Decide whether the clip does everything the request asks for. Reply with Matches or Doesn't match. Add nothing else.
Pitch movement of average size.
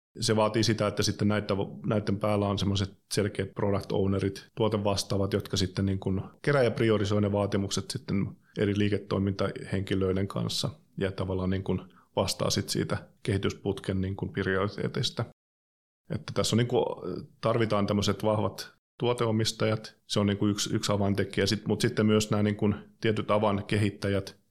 Doesn't match